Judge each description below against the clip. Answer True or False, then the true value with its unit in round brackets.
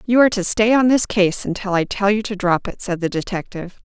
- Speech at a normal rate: False (265 wpm)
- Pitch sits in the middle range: False (200 Hz)